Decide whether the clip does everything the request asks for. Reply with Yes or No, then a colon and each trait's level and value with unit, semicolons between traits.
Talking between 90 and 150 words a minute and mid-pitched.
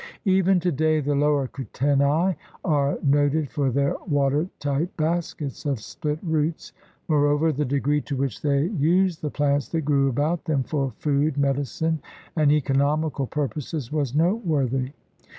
Yes: average, 145 wpm; medium, 145 Hz